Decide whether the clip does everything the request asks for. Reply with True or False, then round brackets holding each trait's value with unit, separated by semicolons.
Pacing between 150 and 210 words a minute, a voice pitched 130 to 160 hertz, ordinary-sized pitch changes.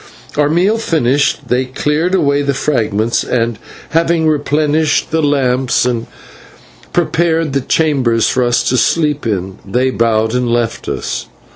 False (140 wpm; 140 Hz; 4.6 semitones)